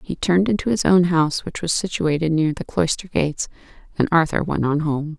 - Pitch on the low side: No, medium, 165 Hz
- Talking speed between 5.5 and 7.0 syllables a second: Yes, 5.7 syllables/s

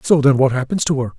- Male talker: Yes, male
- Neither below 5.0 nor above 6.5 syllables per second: No, 6.7 syllables/s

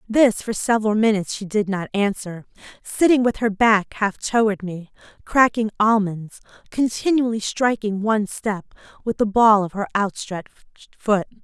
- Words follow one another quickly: No, average, 145 wpm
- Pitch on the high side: Yes, high, 210 Hz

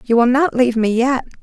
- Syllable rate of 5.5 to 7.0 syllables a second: Yes, 6.0 syllables/s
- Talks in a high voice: Yes, high, 245 Hz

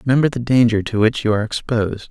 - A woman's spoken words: No, male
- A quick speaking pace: Yes, fast, 230 wpm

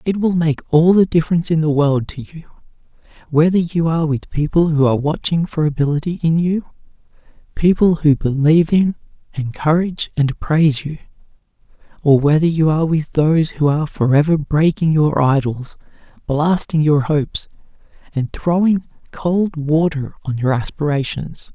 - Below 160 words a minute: Yes, average, 150 wpm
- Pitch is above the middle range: No, medium, 155 Hz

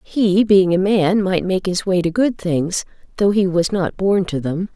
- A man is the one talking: No, female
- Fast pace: Yes, fast, 225 wpm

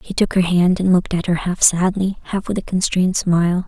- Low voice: No, medium, 180 Hz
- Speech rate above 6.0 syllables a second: No, 5.8 syllables/s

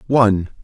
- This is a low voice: Yes, low, 110 Hz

